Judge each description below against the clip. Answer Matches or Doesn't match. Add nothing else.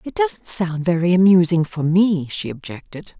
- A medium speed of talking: Matches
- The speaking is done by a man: Doesn't match